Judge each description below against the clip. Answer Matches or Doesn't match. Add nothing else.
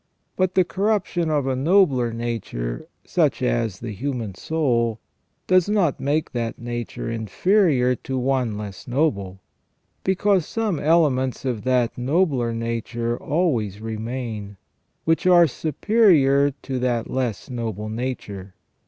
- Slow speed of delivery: Matches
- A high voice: Doesn't match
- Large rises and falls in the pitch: Matches